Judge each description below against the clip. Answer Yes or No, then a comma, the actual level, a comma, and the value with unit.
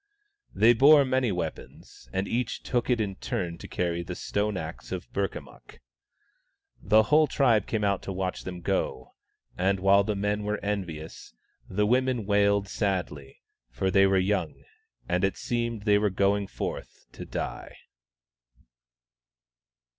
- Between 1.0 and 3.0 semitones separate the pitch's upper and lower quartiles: Yes, average, 2.7 semitones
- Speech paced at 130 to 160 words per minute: Yes, average, 150 wpm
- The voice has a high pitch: No, low, 100 Hz